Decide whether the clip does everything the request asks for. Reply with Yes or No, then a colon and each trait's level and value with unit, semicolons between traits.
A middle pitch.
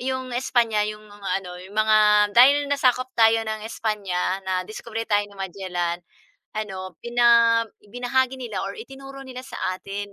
No: high, 220 Hz